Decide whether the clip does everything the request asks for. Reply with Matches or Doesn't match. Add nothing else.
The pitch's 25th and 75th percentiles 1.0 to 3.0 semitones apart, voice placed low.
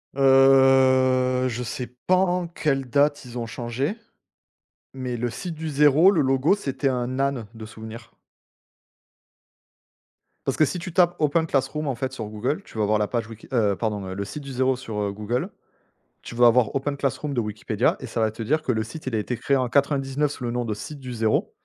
Doesn't match